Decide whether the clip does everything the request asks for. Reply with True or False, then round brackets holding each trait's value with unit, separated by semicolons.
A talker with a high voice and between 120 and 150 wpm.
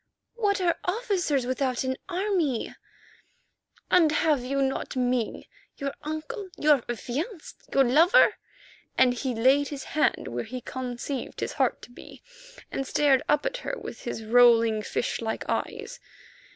True (275 Hz; 145 wpm)